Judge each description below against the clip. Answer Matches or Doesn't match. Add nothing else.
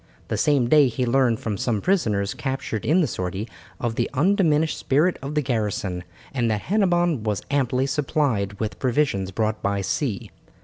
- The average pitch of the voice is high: Doesn't match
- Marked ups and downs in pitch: Matches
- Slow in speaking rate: Doesn't match